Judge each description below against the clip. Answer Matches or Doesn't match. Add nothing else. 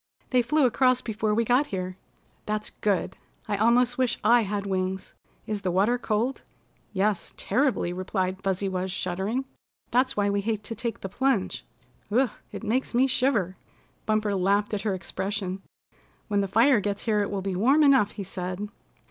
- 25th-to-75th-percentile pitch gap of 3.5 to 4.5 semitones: Matches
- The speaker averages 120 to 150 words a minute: Doesn't match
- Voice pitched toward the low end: Doesn't match